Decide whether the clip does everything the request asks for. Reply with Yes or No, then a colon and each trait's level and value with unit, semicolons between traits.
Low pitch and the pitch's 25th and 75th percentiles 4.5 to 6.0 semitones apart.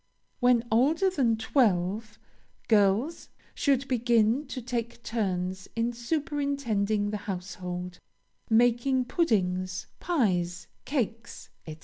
No: high, 230 Hz; average, 4.8 semitones